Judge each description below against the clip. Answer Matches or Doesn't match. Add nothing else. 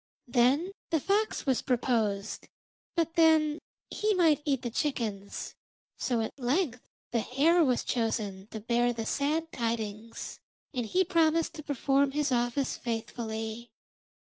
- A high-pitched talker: Matches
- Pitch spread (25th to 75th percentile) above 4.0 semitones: Matches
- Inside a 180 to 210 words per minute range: Doesn't match